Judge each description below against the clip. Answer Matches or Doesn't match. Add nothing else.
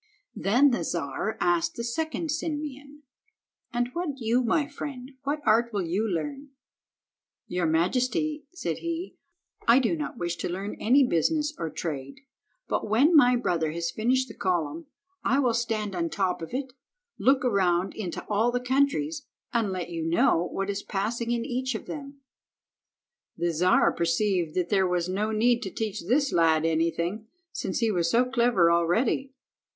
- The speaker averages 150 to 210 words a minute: Matches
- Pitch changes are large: Matches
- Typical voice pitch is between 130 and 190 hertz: Doesn't match